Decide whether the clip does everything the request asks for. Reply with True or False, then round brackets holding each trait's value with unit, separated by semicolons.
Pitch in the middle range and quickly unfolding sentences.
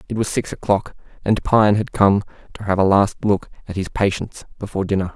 False (100 Hz; 210 wpm)